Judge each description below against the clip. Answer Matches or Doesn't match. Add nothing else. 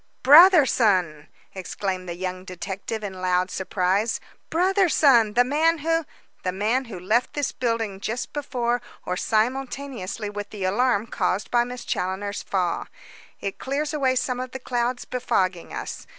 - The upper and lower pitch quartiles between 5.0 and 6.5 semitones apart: Matches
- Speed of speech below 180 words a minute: Matches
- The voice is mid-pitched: Doesn't match